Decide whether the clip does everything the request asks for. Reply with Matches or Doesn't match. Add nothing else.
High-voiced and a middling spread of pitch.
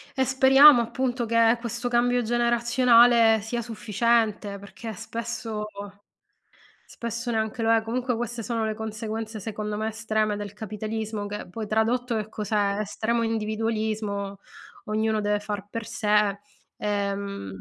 Doesn't match